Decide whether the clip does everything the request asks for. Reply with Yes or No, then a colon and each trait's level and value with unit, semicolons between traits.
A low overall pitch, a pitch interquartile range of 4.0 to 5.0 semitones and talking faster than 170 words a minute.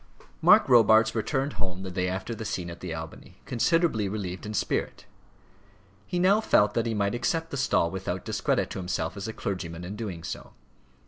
Yes: low, 105 Hz; average, 4.4 semitones; average, 190 wpm